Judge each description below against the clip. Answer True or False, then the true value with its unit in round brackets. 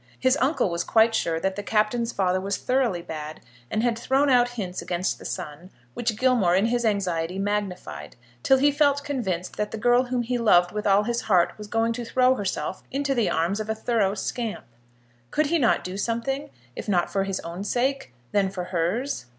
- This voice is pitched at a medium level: False (215 Hz)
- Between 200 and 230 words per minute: True (205 wpm)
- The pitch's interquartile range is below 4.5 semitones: False (4.8 semitones)